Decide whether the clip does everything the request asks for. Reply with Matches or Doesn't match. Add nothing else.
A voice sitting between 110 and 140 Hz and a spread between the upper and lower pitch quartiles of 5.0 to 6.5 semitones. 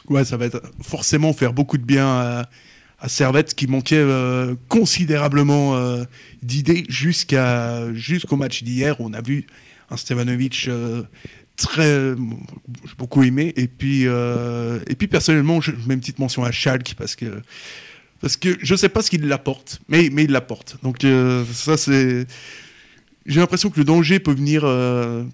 Doesn't match